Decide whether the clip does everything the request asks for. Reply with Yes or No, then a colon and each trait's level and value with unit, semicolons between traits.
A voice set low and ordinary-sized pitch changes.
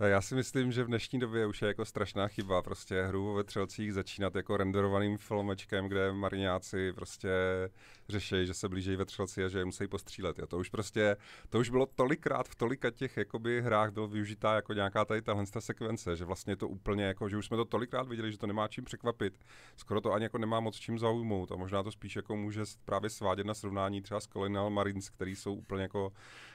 No: low, 105 Hz; narrow, 2.3 semitones